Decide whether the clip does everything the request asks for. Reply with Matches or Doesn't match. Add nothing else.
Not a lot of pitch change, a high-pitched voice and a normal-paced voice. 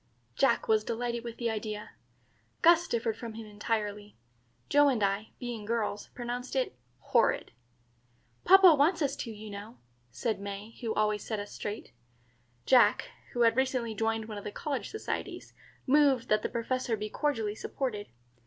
Doesn't match